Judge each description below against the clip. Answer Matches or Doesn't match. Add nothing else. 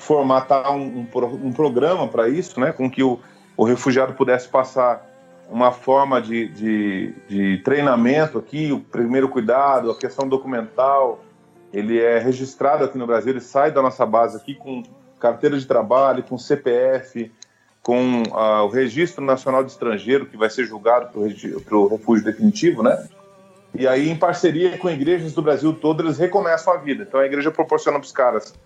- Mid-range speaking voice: Doesn't match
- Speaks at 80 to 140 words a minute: Doesn't match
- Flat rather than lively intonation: Doesn't match